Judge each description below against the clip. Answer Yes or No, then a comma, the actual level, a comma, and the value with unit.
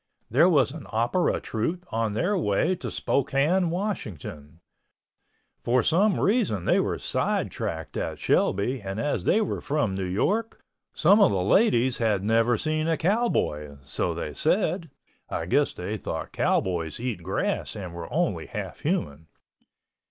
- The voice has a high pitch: No, low, 120 Hz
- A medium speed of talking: Yes, average, 150 wpm